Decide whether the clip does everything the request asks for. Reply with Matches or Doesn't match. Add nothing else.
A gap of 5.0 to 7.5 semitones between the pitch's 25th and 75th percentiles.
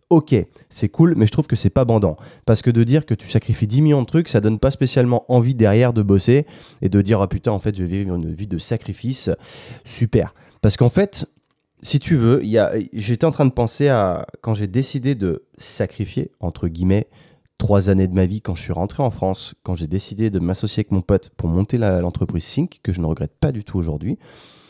Matches